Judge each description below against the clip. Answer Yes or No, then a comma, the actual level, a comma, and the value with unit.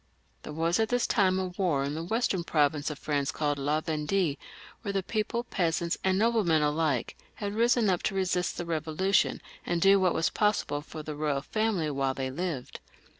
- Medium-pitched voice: Yes, medium, 170 Hz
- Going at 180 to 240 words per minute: Yes, average, 190 wpm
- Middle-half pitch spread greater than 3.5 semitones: Yes, average, 4.7 semitones